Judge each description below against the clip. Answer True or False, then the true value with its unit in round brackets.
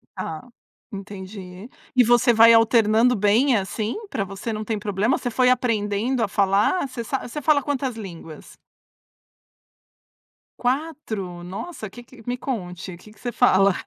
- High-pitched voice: True (220 Hz)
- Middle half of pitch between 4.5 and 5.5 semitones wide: False (4.0 semitones)